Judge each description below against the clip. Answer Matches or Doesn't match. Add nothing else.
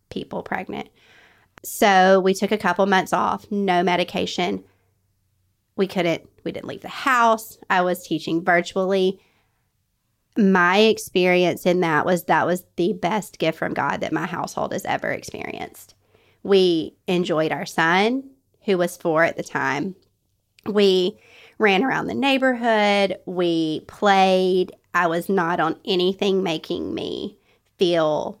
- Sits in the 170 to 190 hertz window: Matches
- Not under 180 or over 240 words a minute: Doesn't match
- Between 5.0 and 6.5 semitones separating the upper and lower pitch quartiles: Doesn't match